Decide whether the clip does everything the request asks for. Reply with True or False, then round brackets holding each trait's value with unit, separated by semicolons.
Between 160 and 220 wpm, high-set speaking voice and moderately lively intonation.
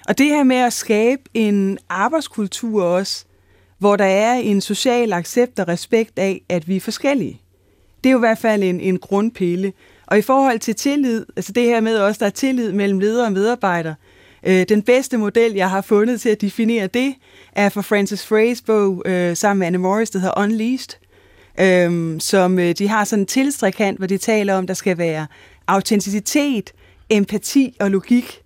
True (190 wpm; 205 Hz; 3.4 semitones)